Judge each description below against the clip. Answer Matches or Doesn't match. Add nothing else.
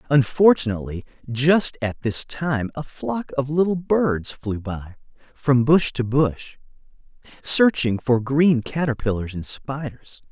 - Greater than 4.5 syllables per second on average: Doesn't match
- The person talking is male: Matches